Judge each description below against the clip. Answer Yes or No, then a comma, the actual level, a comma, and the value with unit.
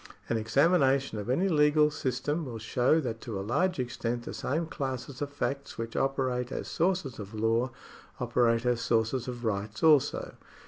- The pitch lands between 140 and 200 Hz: No, low, 125 Hz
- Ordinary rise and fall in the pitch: Yes, average, 3.7 semitones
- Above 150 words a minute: Yes, average, 170 wpm